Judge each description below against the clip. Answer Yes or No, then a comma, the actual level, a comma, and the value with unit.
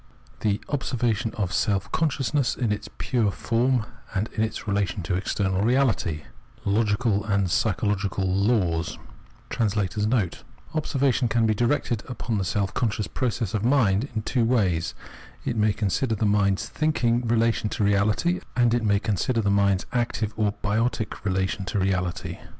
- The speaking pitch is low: Yes, low, 110 Hz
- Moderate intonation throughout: Yes, average, 3.2 semitones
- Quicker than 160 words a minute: No, average, 150 wpm